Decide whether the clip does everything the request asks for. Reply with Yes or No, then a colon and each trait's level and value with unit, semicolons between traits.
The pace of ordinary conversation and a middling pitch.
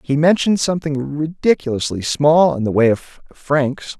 Yes: average, 150 wpm; medium, 145 Hz